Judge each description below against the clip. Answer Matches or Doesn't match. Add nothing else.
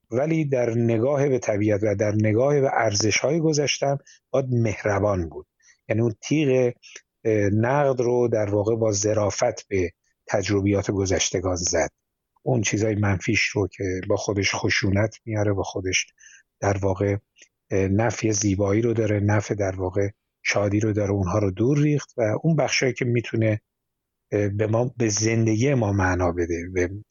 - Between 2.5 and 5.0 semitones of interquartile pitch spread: Matches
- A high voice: Doesn't match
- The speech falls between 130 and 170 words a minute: Matches